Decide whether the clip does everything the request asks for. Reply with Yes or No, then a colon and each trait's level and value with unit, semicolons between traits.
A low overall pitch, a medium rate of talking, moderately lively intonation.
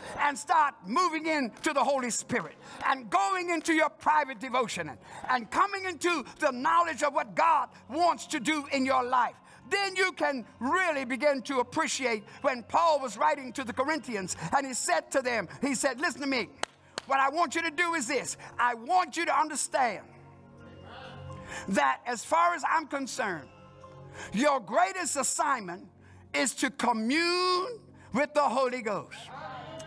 No: very high, 285 Hz; average, 160 wpm; average, 4.4 semitones